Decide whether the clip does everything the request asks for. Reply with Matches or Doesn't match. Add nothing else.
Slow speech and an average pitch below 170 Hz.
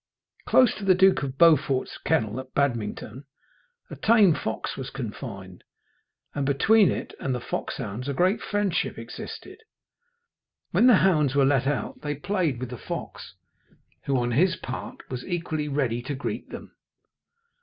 Doesn't match